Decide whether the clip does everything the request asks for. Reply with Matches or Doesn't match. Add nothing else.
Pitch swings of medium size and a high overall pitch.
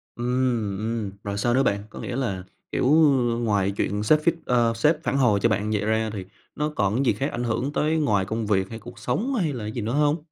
Doesn't match